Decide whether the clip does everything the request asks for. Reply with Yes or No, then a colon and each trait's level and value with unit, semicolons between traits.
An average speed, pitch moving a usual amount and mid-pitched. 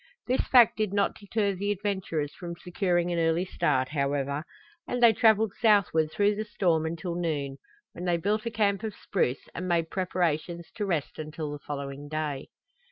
Yes: average, 175 wpm; average, 4.7 semitones; medium, 175 Hz